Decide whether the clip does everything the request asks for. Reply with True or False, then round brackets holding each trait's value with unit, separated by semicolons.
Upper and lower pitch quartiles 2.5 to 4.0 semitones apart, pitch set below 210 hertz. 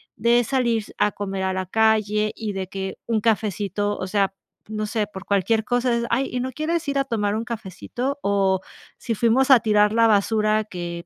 False (2.8 semitones; 215 Hz)